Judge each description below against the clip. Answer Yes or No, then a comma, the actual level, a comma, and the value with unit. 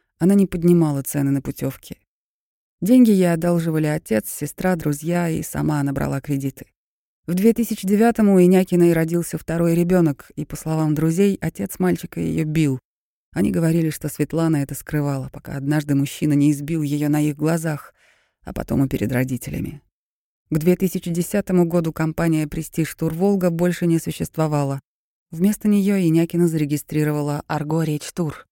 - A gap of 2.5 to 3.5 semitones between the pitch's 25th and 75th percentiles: Yes, average, 2.9 semitones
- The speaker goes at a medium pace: Yes, average, 145 wpm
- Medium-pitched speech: Yes, medium, 160 Hz